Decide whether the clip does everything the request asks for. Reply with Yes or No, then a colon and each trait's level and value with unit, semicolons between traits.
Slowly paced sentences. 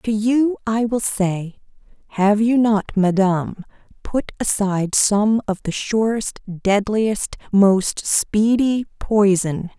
Yes: slow, 115 wpm